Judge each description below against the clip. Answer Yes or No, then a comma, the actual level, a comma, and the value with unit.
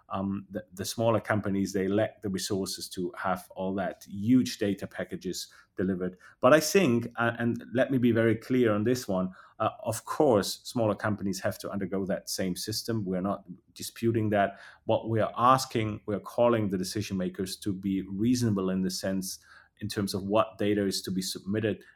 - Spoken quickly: No, average, 190 wpm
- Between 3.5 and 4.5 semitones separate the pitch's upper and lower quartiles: No, average, 2.8 semitones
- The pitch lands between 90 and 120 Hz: Yes, low, 100 Hz